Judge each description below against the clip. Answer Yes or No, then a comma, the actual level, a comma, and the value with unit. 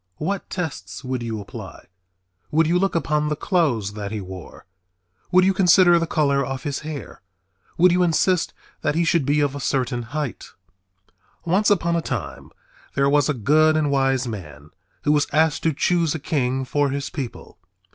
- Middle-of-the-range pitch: Yes, medium, 145 Hz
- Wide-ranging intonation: No, average, 4.2 semitones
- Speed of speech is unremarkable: Yes, average, 180 wpm